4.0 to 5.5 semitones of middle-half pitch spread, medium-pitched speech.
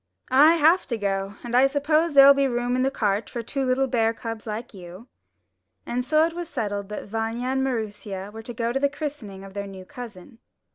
No: average, 4.7 semitones; high, 240 Hz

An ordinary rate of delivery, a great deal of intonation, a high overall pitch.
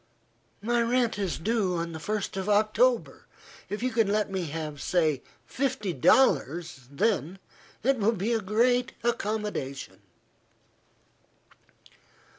No: slow, 120 wpm; wide, 5.7 semitones; high, 205 Hz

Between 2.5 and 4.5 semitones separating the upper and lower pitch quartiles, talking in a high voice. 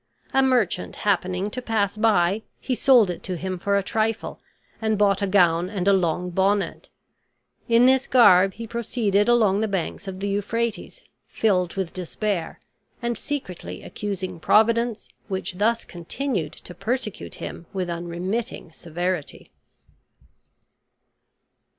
Yes: average, 3.8 semitones; high, 200 Hz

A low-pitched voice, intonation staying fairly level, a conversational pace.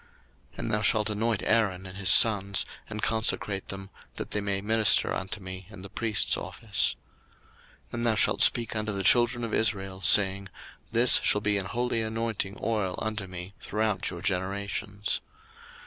Yes: low, 105 Hz; narrow, 2.3 semitones; average, 170 wpm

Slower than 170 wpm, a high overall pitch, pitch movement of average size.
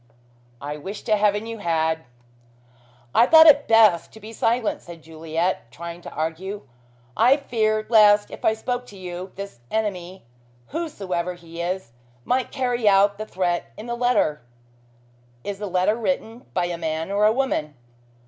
Yes: average, 160 wpm; high, 200 Hz; average, 4.7 semitones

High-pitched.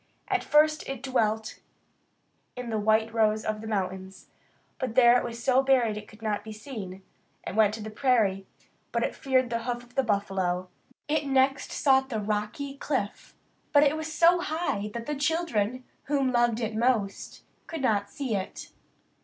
Yes: high, 235 Hz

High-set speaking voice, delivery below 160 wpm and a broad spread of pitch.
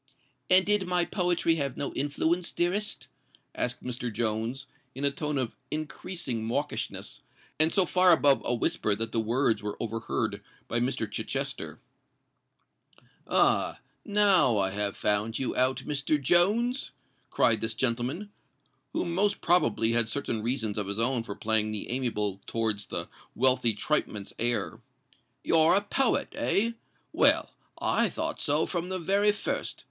No: low, 130 Hz; average, 140 wpm; wide, 7.5 semitones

